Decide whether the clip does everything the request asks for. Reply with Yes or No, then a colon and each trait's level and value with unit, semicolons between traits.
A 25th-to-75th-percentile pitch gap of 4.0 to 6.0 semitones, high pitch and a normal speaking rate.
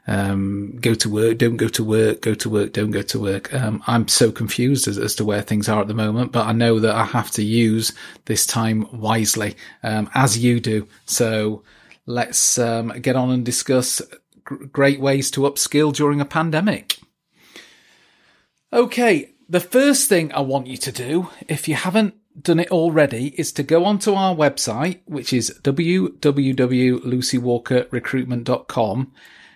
No: average, 5.0 semitones; low, 125 Hz; average, 165 wpm